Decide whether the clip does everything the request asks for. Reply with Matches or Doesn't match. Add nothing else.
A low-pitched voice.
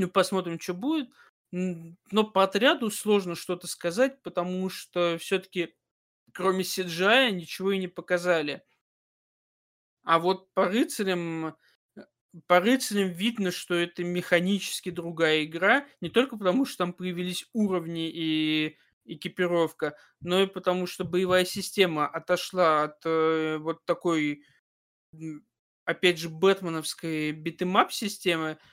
Doesn't match